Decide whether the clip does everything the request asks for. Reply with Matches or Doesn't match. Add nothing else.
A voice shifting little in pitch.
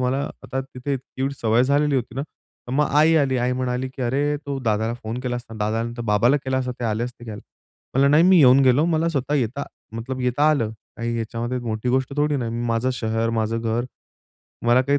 Doesn't match